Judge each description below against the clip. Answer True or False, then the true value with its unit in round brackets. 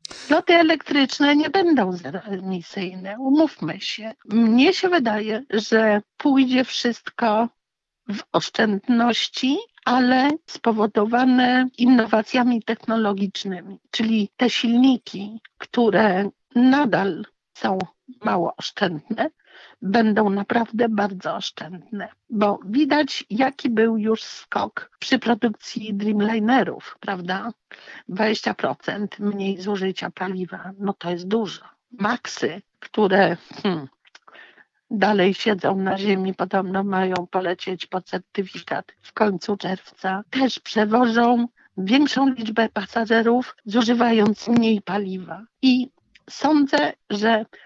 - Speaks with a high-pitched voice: True (220 Hz)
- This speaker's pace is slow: True (95 wpm)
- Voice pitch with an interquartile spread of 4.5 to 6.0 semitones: False (4.1 semitones)